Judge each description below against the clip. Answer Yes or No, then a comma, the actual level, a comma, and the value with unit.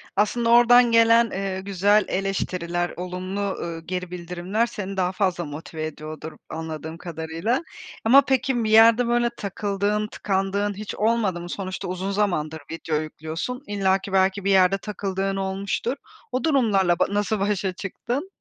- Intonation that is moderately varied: Yes, average, 3.2 semitones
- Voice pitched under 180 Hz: No, high, 195 Hz